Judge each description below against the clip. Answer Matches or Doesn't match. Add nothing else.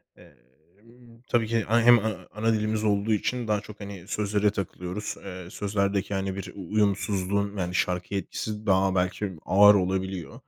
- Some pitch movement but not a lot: Doesn't match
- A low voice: Matches